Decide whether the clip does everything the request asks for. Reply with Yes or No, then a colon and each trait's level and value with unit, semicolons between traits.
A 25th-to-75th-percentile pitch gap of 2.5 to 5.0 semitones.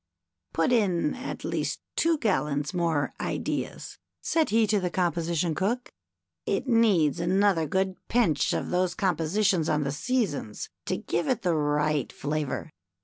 No: wide, 5.4 semitones